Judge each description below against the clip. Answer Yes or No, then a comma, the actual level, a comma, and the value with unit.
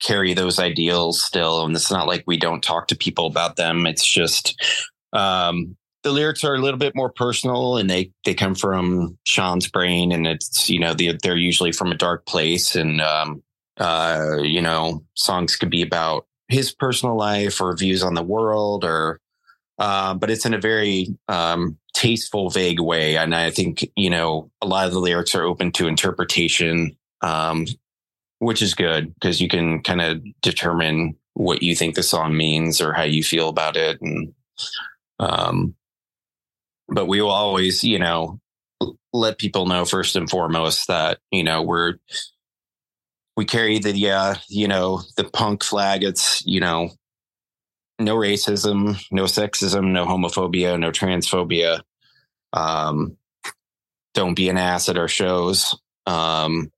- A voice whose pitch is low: Yes, very low, 90 Hz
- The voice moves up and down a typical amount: Yes, average, 3.4 semitones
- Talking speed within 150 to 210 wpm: Yes, average, 165 wpm